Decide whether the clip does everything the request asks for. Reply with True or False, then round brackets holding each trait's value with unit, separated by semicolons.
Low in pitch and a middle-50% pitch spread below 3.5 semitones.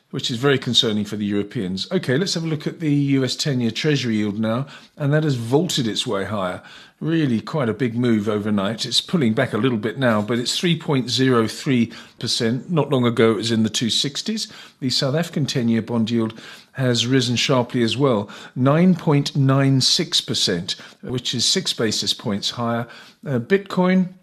False (130 Hz; 4.3 semitones)